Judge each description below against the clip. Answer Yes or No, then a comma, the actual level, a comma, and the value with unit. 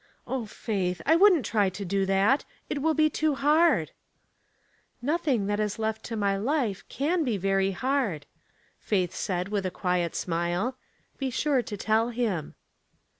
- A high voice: Yes, high, 215 Hz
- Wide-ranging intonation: Yes, wide, 5.9 semitones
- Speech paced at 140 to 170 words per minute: Yes, average, 165 wpm